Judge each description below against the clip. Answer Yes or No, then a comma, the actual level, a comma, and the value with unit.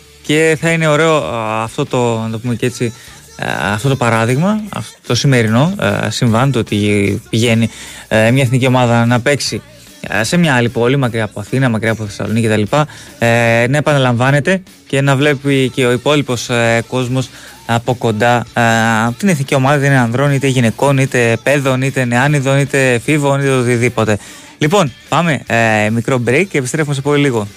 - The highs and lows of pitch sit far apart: No, average, 3.6 semitones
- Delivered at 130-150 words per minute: No, average, 165 wpm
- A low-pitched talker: Yes, low, 125 Hz